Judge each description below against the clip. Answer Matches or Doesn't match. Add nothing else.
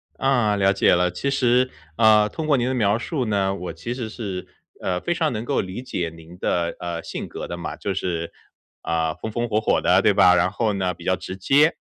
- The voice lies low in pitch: Matches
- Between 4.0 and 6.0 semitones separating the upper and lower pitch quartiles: Matches